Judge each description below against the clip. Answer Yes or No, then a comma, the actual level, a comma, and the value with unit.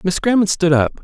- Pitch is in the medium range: Yes, medium, 180 Hz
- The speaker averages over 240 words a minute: No, fast, 230 wpm